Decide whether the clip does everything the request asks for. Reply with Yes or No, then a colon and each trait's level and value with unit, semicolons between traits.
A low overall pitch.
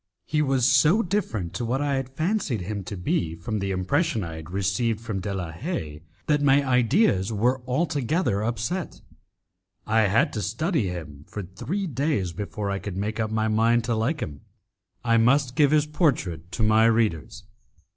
Yes: low, 115 Hz